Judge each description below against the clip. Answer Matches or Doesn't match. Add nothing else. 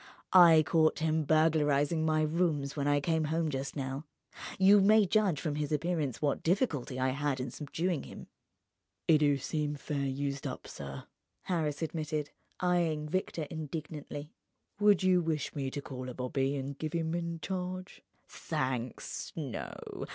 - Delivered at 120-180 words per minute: Matches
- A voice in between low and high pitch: Matches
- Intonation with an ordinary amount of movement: Matches